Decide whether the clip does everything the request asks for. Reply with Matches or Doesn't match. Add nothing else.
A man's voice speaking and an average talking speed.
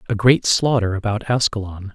Matches